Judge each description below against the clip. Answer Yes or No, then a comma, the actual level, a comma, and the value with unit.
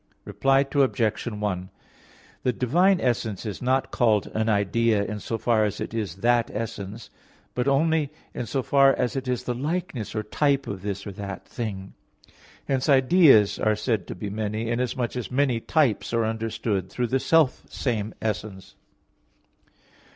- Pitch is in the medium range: No, low, 115 Hz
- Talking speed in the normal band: Yes, average, 160 wpm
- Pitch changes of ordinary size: Yes, average, 3.9 semitones